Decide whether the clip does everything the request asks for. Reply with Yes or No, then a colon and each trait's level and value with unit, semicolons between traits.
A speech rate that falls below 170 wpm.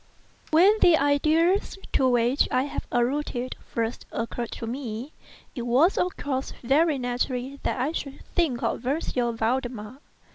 Yes: average, 145 wpm